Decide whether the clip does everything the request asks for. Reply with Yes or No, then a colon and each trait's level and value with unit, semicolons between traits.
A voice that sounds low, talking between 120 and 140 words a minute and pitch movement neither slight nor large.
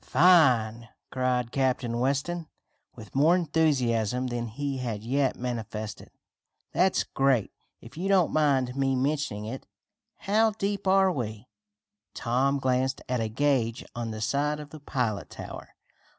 Yes: low, 130 Hz; slow, 135 wpm; average, 4.2 semitones